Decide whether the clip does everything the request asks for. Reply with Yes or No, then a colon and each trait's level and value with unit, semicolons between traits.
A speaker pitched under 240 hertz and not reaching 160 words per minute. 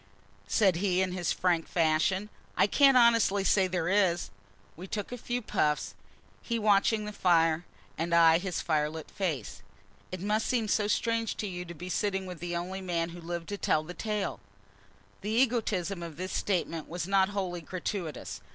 No: medium, 185 Hz; average, 175 wpm